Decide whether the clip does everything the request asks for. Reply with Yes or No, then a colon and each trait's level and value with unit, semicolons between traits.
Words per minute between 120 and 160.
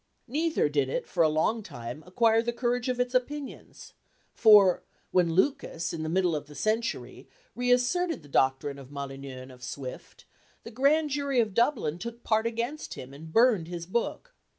No: average, 175 wpm